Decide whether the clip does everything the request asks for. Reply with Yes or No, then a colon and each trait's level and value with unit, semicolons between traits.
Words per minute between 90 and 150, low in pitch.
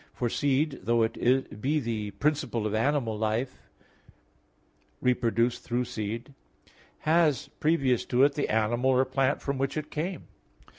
Yes: average, 140 wpm; low, 125 Hz